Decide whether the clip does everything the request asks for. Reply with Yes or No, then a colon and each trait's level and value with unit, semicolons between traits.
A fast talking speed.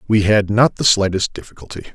No: average, 185 wpm